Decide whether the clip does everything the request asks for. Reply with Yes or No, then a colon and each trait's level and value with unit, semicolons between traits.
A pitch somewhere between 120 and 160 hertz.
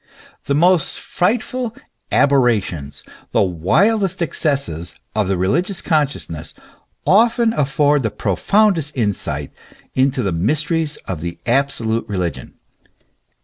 Yes: low, 135 Hz